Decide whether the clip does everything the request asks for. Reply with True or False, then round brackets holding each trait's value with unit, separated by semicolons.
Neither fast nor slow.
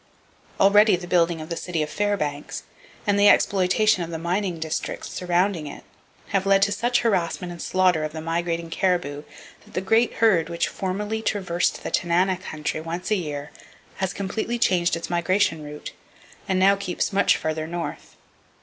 True (170 wpm)